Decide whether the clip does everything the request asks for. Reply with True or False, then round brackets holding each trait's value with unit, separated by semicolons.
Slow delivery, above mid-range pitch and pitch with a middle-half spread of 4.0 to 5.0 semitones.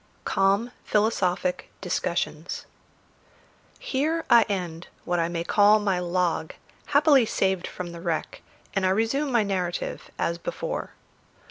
True (125 wpm; 195 Hz; 4.6 semitones)